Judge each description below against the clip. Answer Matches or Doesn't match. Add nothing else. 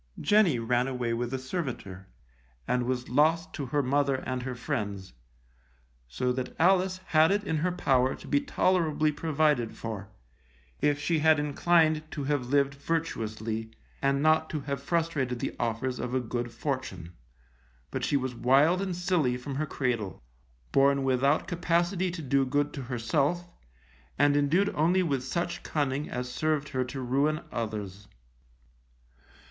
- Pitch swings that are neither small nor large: Matches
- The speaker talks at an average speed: Matches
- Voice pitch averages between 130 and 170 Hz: Matches